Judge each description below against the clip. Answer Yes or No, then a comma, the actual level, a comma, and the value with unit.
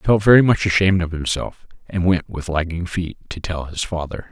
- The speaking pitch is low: Yes, very low, 90 Hz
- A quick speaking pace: Yes, fast, 220 wpm